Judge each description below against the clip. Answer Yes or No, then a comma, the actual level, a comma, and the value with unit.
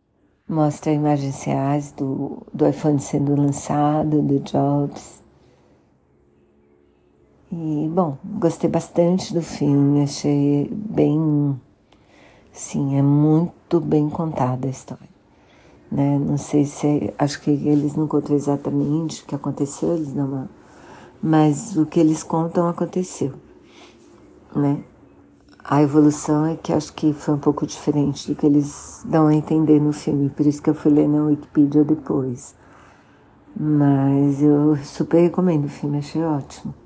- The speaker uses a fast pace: No, average, 135 wpm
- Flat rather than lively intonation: Yes, narrow, 1.6 semitones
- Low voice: No, medium, 150 Hz